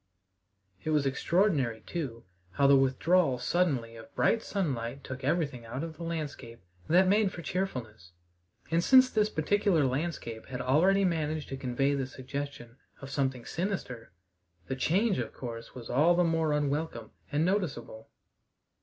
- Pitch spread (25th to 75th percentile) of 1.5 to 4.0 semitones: No, average, 5.3 semitones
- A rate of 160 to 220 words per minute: No, average, 150 wpm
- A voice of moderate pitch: Yes, medium, 145 Hz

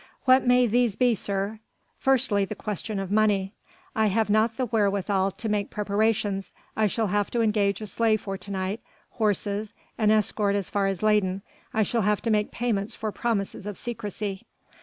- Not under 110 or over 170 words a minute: No, average, 180 wpm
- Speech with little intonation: Yes, narrow, 1.8 semitones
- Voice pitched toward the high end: Yes, high, 210 Hz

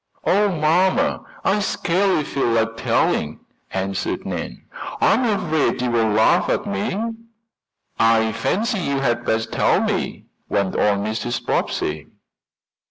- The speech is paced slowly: Yes, slow, 125 wpm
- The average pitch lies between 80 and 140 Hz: Yes, low, 135 Hz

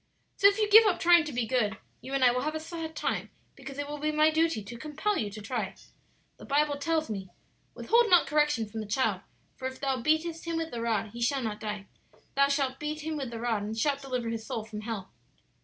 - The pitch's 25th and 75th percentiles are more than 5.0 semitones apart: Yes, wide, 5.5 semitones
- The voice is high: Yes, very high, 270 Hz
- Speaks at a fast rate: Yes, fast, 245 wpm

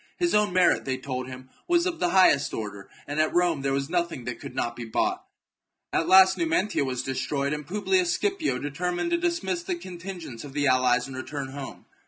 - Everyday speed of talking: No, fast, 210 wpm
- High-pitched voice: No, medium, 155 Hz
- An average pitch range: No, wide, 6.2 semitones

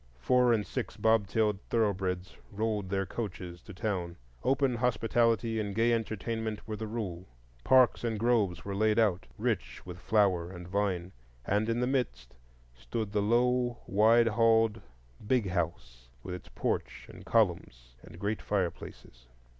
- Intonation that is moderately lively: Yes, average, 3.8 semitones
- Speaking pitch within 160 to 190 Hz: No, low, 105 Hz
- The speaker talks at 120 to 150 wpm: Yes, average, 145 wpm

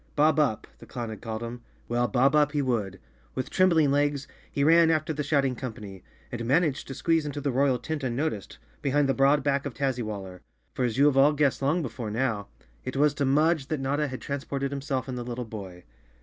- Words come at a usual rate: No, fast, 220 wpm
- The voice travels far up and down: No, average, 3.4 semitones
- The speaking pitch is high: No, low, 135 Hz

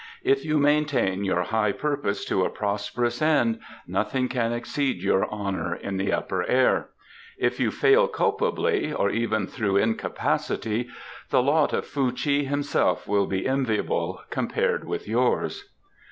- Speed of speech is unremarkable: Yes, average, 145 wpm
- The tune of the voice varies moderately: No, wide, 5.9 semitones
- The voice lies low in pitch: Yes, low, 120 Hz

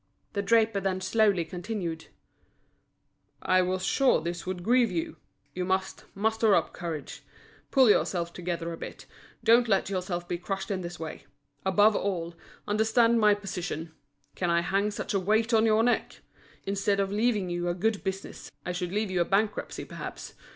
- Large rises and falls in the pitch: No, average, 3.4 semitones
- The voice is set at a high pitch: Yes, high, 195 Hz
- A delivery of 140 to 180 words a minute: Yes, average, 170 wpm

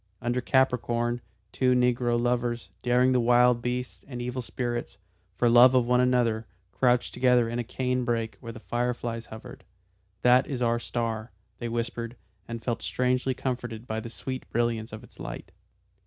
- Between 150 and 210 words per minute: Yes, average, 170 wpm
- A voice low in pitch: Yes, low, 120 Hz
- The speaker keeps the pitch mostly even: Yes, narrow, 1.1 semitones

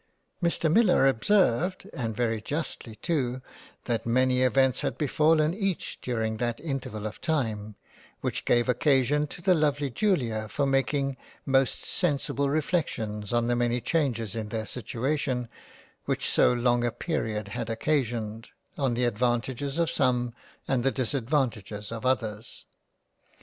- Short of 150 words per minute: Yes, average, 140 wpm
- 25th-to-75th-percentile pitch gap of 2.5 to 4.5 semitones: Yes, average, 4.0 semitones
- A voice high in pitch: No, low, 125 Hz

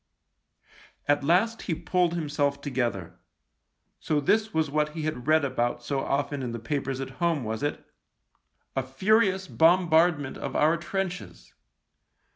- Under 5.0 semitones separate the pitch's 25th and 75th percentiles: Yes, average, 4.2 semitones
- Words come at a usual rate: Yes, average, 150 wpm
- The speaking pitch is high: No, medium, 150 Hz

